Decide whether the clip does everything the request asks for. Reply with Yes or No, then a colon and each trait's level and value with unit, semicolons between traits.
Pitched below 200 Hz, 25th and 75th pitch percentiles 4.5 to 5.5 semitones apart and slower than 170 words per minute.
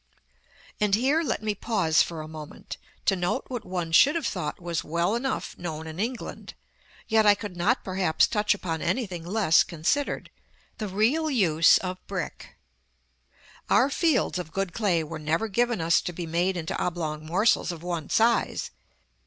No: medium, 185 Hz; average, 5.2 semitones; average, 175 wpm